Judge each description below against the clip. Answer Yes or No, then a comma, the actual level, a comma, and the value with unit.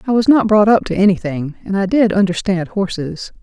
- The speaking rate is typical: No, fast, 210 wpm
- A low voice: No, high, 195 Hz